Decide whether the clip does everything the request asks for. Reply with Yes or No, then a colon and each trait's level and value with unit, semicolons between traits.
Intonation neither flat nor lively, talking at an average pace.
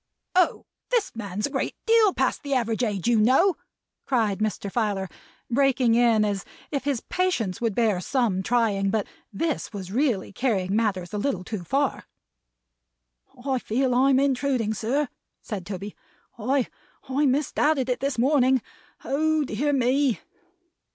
Yes: average, 4.7 semitones; average, 145 wpm